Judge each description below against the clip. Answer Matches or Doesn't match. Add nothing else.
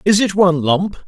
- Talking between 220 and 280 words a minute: Matches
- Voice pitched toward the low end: Doesn't match